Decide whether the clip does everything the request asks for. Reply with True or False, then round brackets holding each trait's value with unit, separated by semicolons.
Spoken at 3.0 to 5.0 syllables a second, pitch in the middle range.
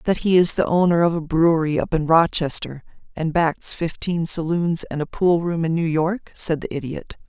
True (4.9 syllables/s; 165 Hz)